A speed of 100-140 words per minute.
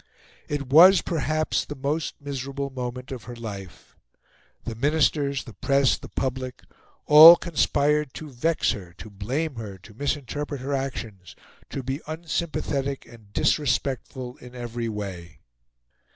Yes: slow, 135 wpm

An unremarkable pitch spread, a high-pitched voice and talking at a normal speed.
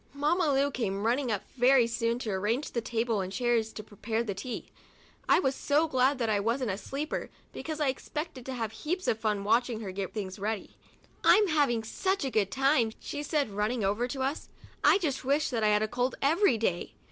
No: average, 4.6 semitones; high, 240 Hz; fast, 220 wpm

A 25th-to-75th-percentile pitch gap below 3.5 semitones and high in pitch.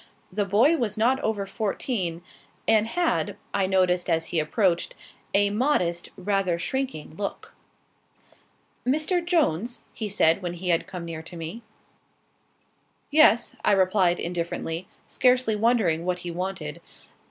No: average, 5.1 semitones; high, 195 Hz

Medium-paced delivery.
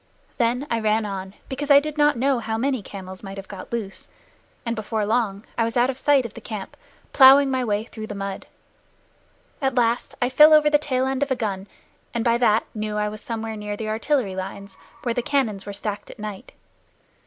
No: fast, 215 wpm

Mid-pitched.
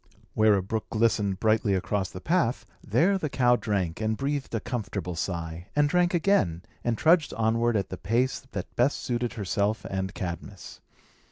No: low, 110 Hz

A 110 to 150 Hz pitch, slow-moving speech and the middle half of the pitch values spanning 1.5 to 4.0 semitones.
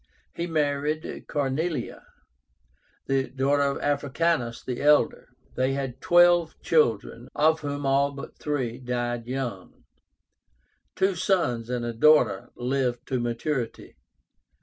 Yes: low, 135 Hz; slow, 115 wpm; average, 3.7 semitones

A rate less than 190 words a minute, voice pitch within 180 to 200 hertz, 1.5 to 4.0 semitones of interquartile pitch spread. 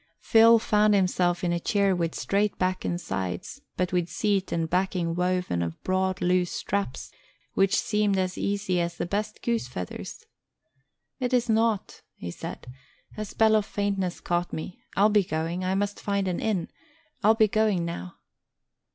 Yes: average, 170 wpm; medium, 185 Hz; average, 3.2 semitones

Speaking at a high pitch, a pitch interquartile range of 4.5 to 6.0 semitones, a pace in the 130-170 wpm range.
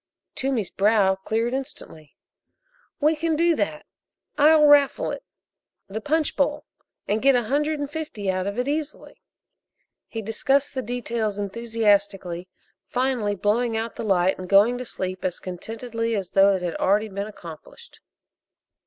Yes: high, 225 Hz; wide, 5.6 semitones; average, 150 wpm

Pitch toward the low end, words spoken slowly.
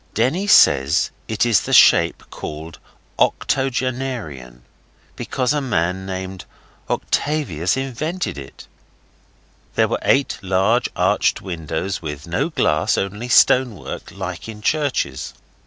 Yes: low, 100 Hz; slow, 115 wpm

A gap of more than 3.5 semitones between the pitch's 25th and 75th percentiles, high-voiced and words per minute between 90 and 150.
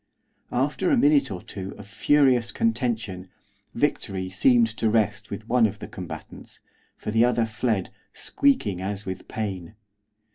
No: average, 4.0 semitones; low, 110 Hz; average, 145 wpm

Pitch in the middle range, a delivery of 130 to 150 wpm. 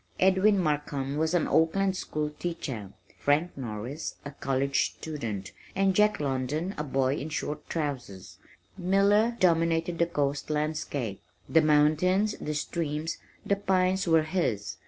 Yes: medium, 155 Hz; slow, 135 wpm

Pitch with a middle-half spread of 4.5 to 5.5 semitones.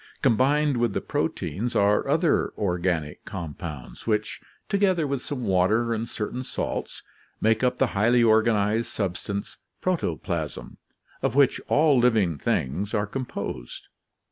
Yes: average, 4.8 semitones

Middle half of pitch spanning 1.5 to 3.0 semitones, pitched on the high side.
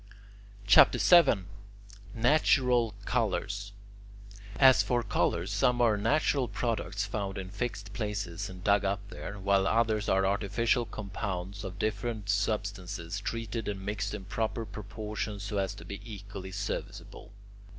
No: narrow, 2.4 semitones; low, 105 Hz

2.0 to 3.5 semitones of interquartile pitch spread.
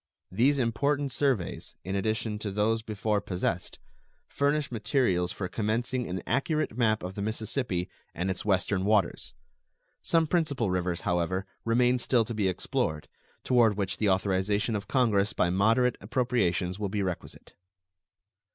No: average, 4.5 semitones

